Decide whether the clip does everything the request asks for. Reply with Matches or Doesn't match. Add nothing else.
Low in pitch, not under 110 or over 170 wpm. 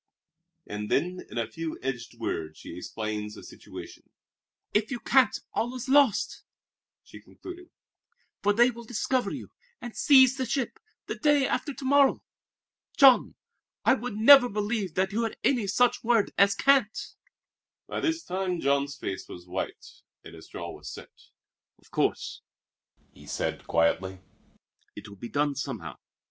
Doesn't match